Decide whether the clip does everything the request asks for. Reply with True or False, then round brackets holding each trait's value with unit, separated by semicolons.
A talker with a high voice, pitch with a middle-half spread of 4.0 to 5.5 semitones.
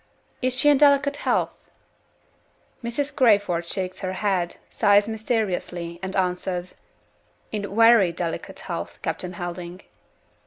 True (195 Hz; 4.3 semitones)